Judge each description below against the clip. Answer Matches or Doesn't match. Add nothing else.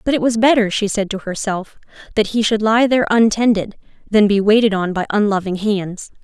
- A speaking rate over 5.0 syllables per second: Matches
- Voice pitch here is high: Matches